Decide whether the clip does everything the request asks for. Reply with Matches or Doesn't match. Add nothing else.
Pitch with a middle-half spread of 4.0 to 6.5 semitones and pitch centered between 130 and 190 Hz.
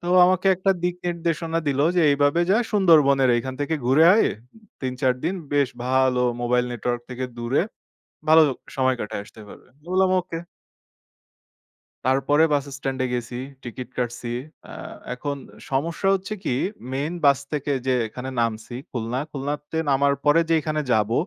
Matches